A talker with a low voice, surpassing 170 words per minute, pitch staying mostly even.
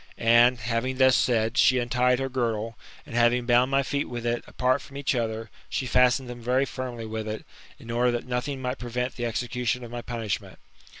Yes: low, 120 Hz; average, 200 wpm; narrow, 1.4 semitones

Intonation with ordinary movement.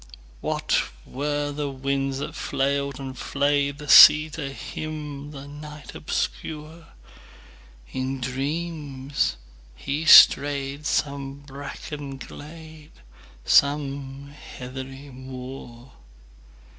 No: narrow, 1.8 semitones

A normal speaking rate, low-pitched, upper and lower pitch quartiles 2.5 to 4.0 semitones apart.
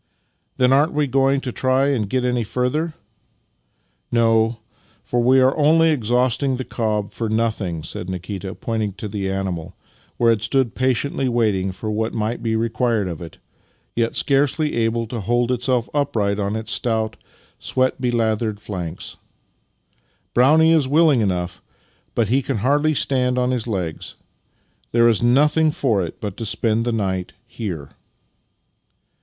Yes: average, 160 wpm; low, 115 Hz; average, 3.7 semitones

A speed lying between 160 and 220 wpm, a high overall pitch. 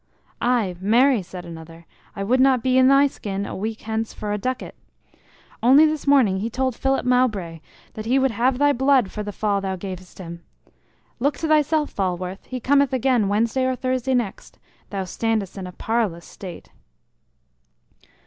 Yes: average, 175 wpm; high, 225 Hz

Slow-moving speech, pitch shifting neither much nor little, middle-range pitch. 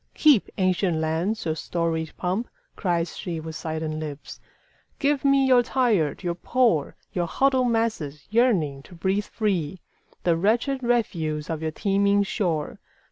No: slow, 130 wpm; wide, 6.4 semitones; medium, 180 Hz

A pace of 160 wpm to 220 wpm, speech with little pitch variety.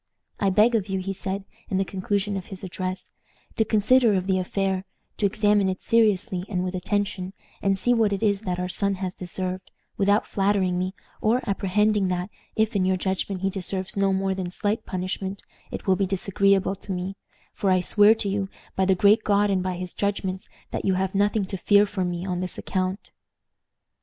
Yes: average, 200 wpm; narrow, 1.7 semitones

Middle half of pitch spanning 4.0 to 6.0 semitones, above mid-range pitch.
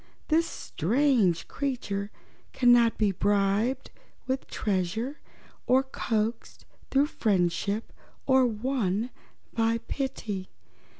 Yes: average, 4.7 semitones; high, 225 Hz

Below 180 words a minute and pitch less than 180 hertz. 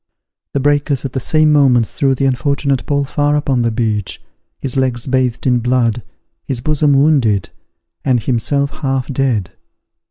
Yes: average, 155 wpm; low, 135 Hz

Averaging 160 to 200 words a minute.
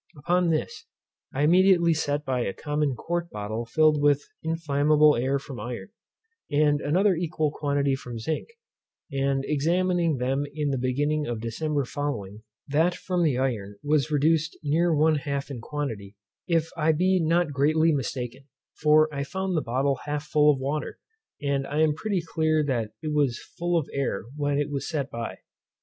Yes: average, 170 wpm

